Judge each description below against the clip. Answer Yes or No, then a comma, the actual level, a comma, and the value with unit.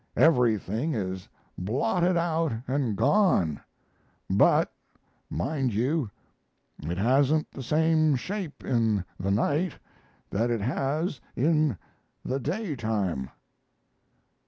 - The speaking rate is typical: No, slow, 95 wpm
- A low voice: Yes, low, 130 Hz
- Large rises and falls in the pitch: Yes, wide, 6.4 semitones